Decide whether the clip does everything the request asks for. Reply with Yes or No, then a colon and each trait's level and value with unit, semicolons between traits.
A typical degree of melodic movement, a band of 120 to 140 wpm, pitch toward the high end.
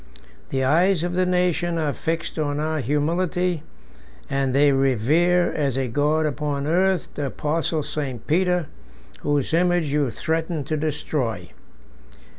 No: average, 3.4 semitones; slow, 135 wpm; medium, 155 Hz